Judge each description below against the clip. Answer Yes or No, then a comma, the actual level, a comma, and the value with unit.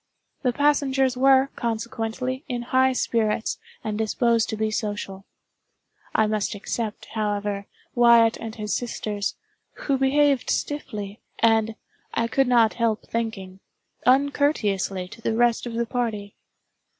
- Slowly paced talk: Yes, slow, 125 wpm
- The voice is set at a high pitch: Yes, high, 230 Hz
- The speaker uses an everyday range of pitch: Yes, average, 3.1 semitones